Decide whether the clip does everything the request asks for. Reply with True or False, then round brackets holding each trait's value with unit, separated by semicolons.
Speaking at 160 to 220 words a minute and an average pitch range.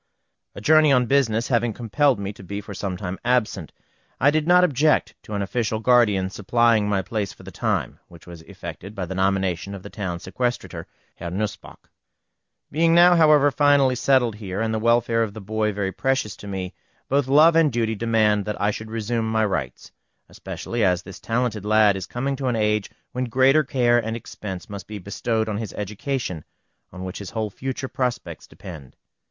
True (190 wpm; 4.1 semitones)